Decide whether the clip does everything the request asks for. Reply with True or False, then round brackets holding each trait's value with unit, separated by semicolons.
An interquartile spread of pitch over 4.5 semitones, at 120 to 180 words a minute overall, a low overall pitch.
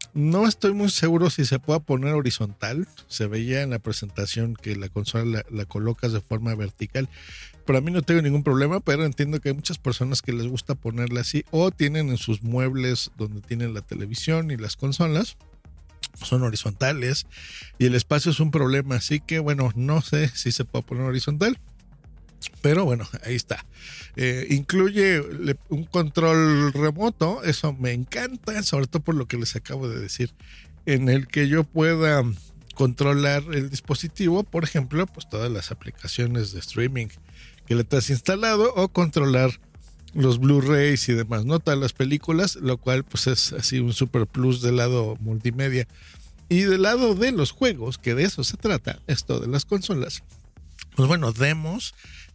True (5.0 semitones; 170 wpm; 130 Hz)